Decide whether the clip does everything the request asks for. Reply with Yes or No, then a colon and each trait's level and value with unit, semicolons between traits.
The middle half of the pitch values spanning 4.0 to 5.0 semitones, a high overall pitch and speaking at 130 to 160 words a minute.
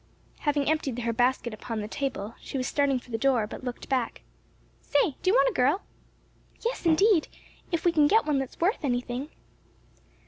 No: average, 4.4 semitones; very high, 275 Hz; average, 185 wpm